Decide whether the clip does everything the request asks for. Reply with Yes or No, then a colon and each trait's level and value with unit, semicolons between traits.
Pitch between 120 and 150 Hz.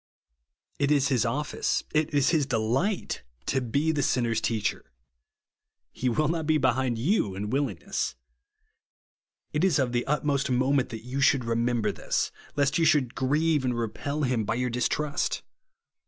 Yes: low, 135 Hz